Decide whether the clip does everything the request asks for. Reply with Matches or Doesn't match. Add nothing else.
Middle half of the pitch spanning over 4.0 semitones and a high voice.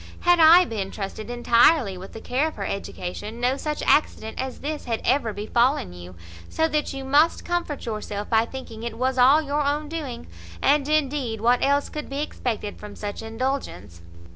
Matches